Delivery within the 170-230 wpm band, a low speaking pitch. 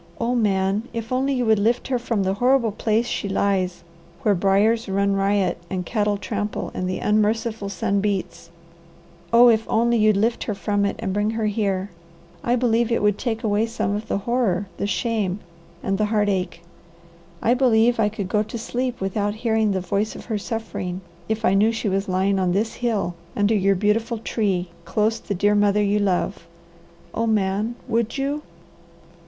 No: average, 185 wpm; high, 210 Hz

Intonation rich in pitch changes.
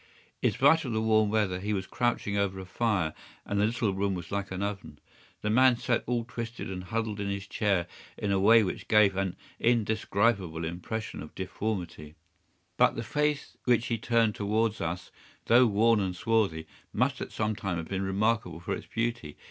No: average, 3.2 semitones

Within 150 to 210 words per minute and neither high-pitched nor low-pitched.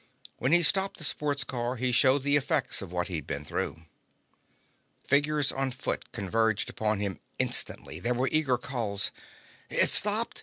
No: average, 160 wpm; low, 130 Hz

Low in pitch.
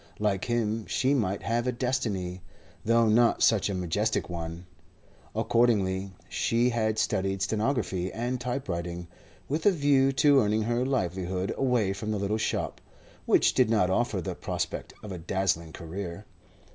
Yes: low, 105 Hz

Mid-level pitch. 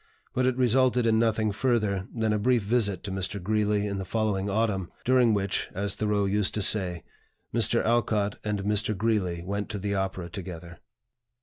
No: low, 105 Hz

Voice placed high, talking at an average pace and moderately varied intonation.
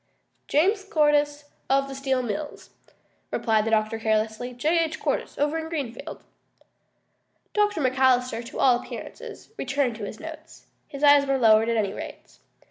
Yes: very high, 270 Hz; average, 150 wpm; average, 4.6 semitones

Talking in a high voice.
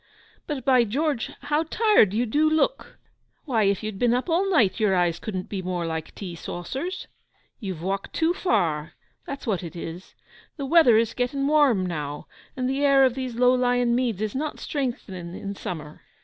Yes: high, 235 Hz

